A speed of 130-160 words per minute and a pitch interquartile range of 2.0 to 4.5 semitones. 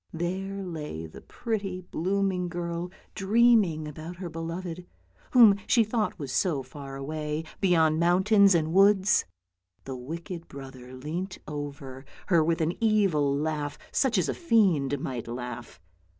No: average, 140 wpm; average, 4.9 semitones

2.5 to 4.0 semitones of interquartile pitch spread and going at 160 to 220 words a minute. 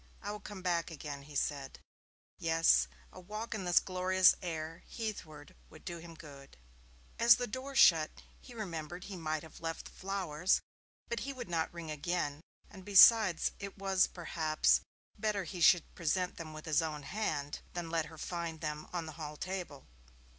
Yes: average, 3.5 semitones; average, 175 wpm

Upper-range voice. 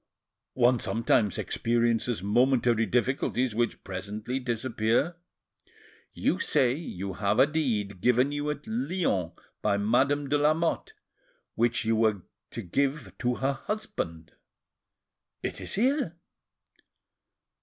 No: low, 120 Hz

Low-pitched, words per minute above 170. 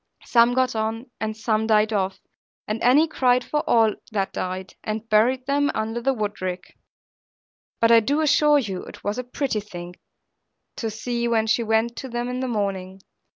No: high, 225 Hz; average, 180 wpm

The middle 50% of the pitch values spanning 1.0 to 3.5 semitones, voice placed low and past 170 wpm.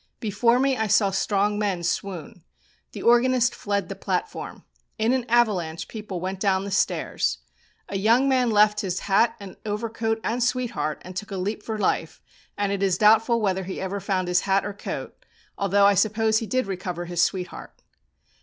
No: average, 2.9 semitones; high, 205 Hz; average, 180 wpm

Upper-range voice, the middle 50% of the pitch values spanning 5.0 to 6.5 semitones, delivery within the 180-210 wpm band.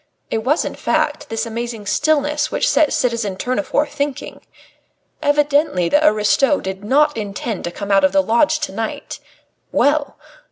No: very high, 270 Hz; wide, 5.5 semitones; average, 155 wpm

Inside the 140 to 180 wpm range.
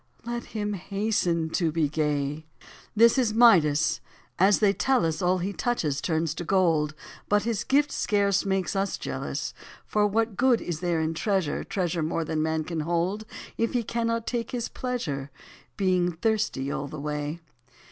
Yes: average, 165 wpm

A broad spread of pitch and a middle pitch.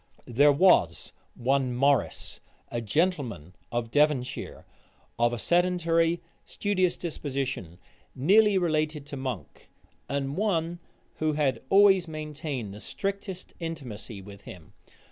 Yes: wide, 5.9 semitones; medium, 145 Hz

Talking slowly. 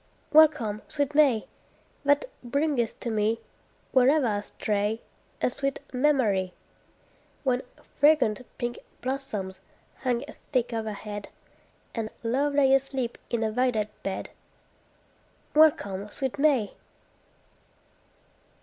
Yes: slow, 100 wpm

